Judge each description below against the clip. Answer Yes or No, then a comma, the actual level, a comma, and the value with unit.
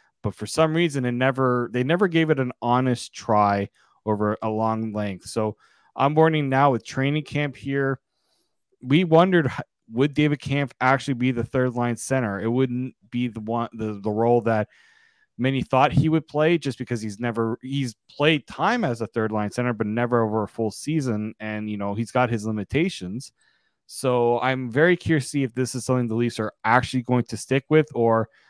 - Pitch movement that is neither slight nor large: Yes, average, 3.7 semitones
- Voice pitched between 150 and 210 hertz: No, low, 125 Hz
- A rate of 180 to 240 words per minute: Yes, average, 200 wpm